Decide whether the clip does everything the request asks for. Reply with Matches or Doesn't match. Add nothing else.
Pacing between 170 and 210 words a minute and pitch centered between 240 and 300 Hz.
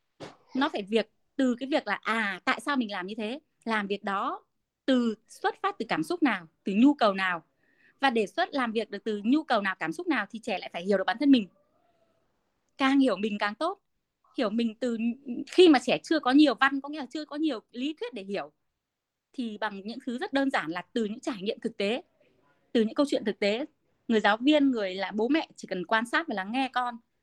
Doesn't match